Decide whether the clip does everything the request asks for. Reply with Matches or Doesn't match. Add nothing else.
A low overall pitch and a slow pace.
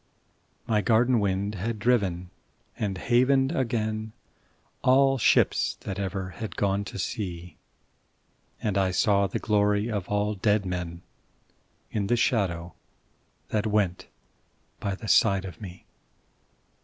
Matches